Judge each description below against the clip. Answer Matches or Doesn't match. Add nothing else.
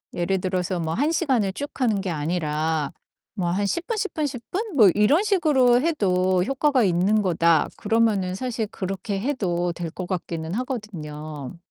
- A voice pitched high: Matches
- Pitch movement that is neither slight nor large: Doesn't match